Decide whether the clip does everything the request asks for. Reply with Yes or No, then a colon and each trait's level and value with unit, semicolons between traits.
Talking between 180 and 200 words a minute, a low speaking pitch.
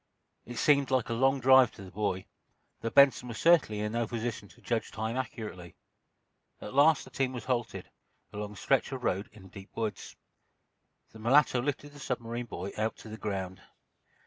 Yes: average, 190 wpm; low, 115 Hz